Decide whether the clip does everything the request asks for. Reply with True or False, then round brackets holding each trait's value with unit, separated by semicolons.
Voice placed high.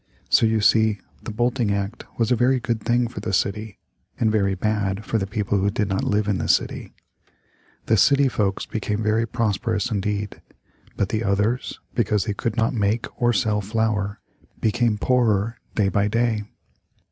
False (110 Hz)